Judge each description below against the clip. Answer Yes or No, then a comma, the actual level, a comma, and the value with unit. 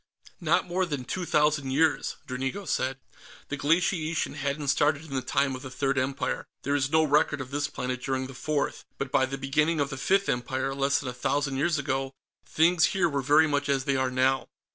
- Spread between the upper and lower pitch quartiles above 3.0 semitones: No, narrow, 2.4 semitones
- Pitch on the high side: No, medium, 140 Hz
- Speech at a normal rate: No, fast, 210 wpm